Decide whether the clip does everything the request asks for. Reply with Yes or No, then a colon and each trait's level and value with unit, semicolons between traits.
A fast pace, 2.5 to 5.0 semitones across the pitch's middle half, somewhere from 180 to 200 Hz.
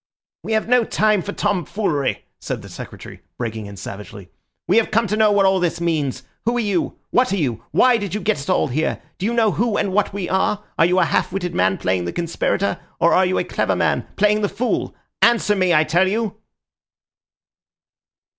Yes: fast, 210 wpm; average, 4.7 semitones; high, 190 Hz